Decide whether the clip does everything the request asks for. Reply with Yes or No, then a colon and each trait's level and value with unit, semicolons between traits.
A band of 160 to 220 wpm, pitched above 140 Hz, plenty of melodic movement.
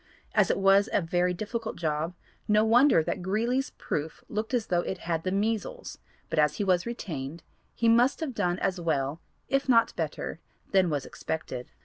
Yes: average, 180 wpm; high, 190 Hz; wide, 5.7 semitones